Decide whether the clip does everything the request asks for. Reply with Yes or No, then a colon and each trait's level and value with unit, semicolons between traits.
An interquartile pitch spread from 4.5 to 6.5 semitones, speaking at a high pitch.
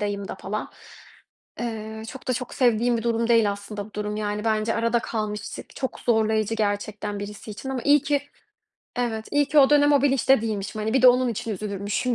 No: average, 3.0 semitones; high, 220 Hz